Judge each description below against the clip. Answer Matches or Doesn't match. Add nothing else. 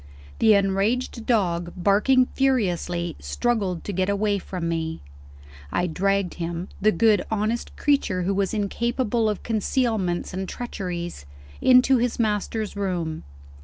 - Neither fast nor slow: Doesn't match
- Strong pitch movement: Doesn't match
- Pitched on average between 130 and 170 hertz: Doesn't match